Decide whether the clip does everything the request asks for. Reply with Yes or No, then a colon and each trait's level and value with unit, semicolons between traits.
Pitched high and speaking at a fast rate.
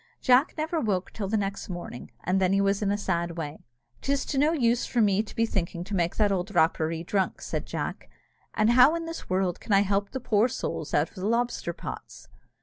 Yes: high, 200 Hz; fast, 220 wpm